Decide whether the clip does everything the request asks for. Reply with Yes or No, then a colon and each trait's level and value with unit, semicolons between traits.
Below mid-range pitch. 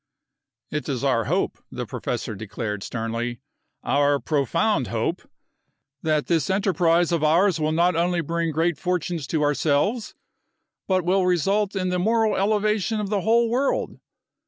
No: medium, 170 Hz